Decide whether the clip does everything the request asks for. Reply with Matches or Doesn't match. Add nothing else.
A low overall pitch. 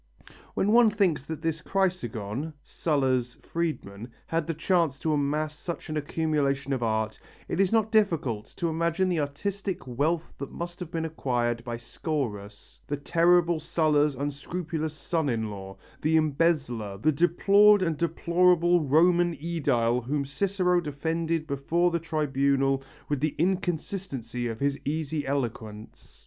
Doesn't match